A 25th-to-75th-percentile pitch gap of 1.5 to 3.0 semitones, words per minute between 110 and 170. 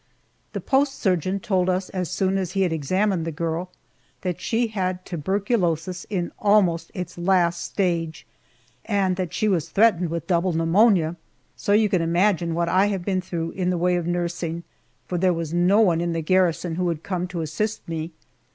No: narrow, 2.4 semitones; average, 190 wpm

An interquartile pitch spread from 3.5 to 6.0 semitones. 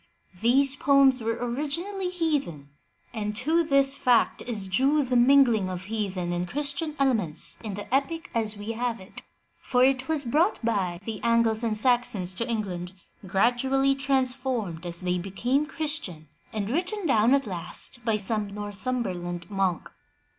Yes: wide, 5.5 semitones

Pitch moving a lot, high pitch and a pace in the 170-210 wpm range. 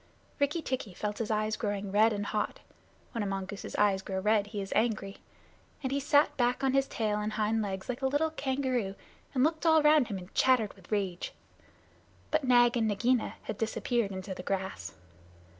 No: average, 4.4 semitones; high, 220 Hz; average, 190 wpm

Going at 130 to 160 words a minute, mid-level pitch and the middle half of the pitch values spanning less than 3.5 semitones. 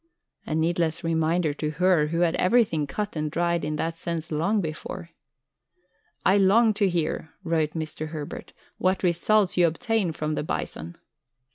Yes: average, 155 wpm; medium, 165 Hz; average, 3.0 semitones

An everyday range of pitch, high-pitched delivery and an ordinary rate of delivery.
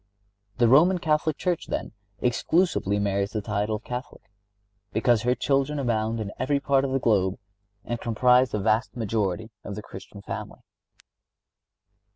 No: average, 4.2 semitones; low, 115 Hz; average, 150 wpm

